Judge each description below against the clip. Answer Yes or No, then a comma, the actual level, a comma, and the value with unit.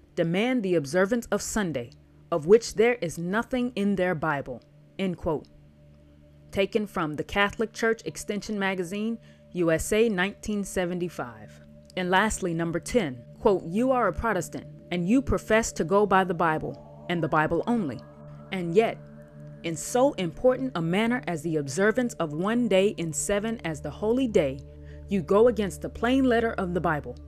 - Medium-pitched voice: Yes, medium, 180 Hz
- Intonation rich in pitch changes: Yes, wide, 6.2 semitones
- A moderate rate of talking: Yes, average, 160 wpm